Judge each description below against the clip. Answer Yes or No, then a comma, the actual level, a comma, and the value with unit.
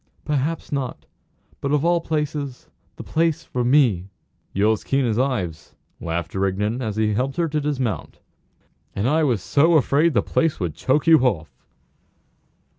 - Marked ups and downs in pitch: Yes, wide, 6.1 semitones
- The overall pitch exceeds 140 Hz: No, low, 130 Hz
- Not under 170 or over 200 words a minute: No, average, 160 wpm